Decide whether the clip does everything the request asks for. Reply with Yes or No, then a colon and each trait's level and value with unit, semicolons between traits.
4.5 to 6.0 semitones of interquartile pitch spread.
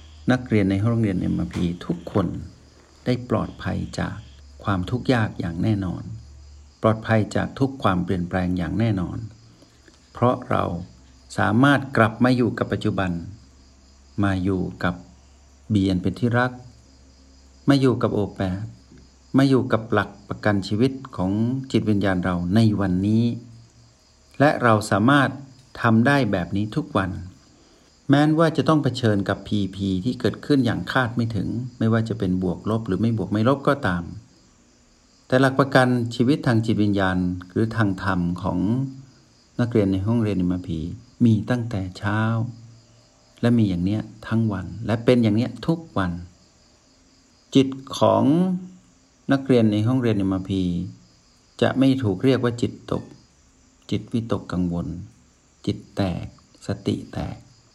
Yes: average, 4.9 semitones